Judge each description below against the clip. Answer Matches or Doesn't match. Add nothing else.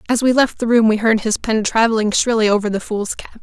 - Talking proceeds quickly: Matches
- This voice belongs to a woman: Matches